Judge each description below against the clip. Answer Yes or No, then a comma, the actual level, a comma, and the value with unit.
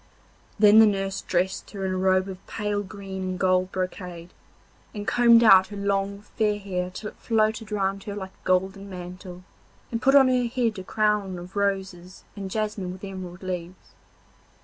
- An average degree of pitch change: No, narrow, 2.2 semitones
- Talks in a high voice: Yes, high, 195 Hz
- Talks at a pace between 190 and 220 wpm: No, average, 180 wpm